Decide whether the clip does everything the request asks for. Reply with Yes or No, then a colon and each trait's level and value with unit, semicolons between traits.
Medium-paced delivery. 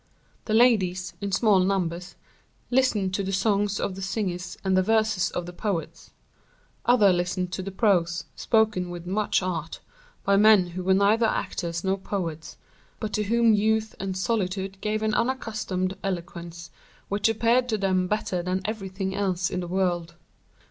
Yes: average, 160 wpm